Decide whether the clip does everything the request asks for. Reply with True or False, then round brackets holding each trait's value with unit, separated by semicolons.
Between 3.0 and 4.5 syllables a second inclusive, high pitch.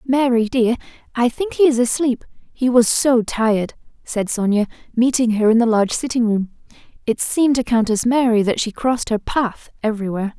True (3.5 syllables/s; 235 Hz)